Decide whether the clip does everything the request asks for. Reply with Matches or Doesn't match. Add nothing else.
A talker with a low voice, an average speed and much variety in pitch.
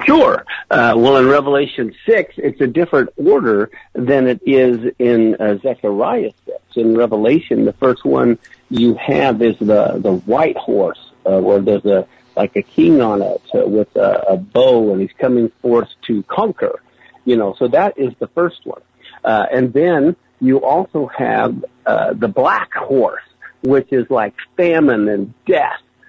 Matches